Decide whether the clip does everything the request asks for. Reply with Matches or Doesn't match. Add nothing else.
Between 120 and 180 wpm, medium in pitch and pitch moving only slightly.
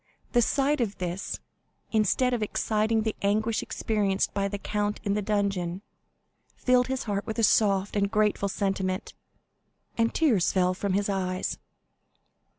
Doesn't match